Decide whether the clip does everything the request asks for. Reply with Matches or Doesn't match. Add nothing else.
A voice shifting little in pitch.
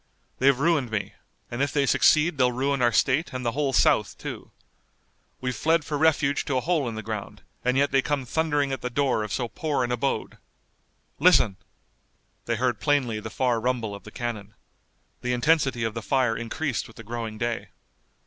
Doesn't match